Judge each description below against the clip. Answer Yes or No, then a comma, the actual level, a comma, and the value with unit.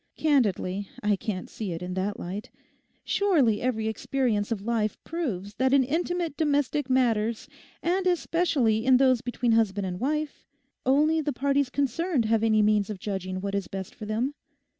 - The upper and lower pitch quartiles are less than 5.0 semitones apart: No, wide, 5.5 semitones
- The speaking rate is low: No, average, 165 wpm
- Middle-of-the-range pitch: No, high, 235 Hz